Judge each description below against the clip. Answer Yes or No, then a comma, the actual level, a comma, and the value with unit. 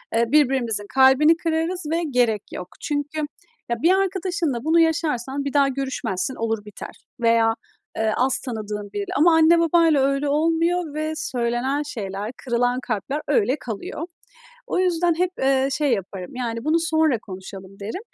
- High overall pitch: Yes, very high, 270 Hz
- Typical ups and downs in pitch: No, wide, 5.9 semitones